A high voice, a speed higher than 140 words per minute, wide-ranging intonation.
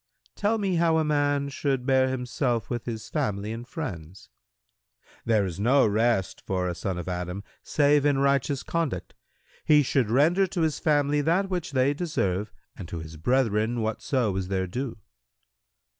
No: low, 125 Hz; average, 165 wpm; wide, 6.0 semitones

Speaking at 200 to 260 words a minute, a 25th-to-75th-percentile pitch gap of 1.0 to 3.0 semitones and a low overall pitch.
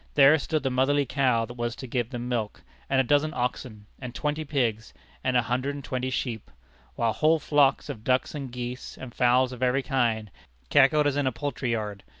Yes: fast, 205 wpm; narrow, 2.6 semitones; low, 130 Hz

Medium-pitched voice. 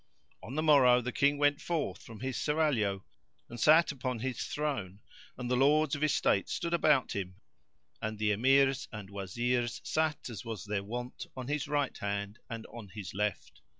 No: low, 125 Hz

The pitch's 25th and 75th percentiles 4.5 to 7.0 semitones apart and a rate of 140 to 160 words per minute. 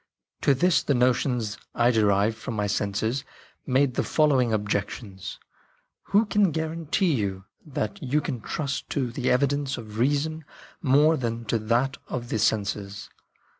Yes: average, 5.0 semitones; average, 155 wpm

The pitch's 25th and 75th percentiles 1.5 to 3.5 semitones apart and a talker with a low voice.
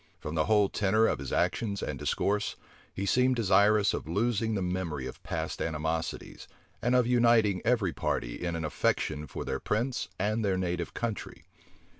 No: average, 4.6 semitones; low, 100 Hz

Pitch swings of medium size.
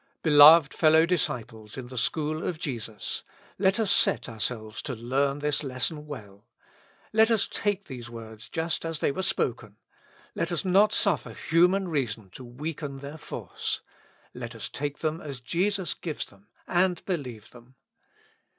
No: wide, 5.8 semitones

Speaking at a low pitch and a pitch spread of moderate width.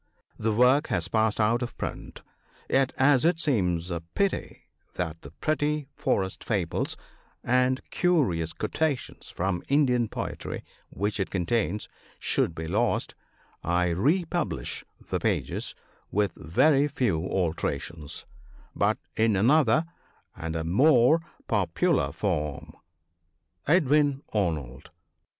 No: low, 110 Hz; wide, 8.3 semitones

